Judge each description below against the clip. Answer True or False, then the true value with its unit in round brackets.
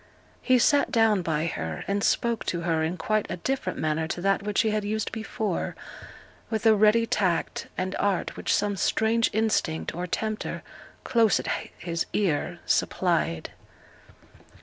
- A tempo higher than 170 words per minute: False (155 wpm)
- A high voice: True (200 Hz)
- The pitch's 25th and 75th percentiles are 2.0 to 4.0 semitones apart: False (4.4 semitones)